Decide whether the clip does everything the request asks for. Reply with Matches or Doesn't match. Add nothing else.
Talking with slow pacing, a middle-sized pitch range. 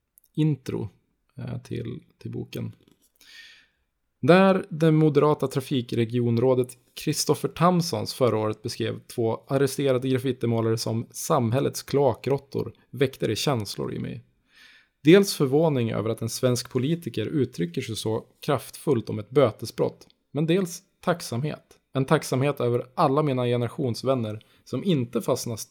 Matches